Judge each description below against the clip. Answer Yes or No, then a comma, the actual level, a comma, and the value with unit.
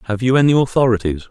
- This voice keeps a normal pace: Yes, average, 185 wpm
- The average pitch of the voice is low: Yes, low, 120 Hz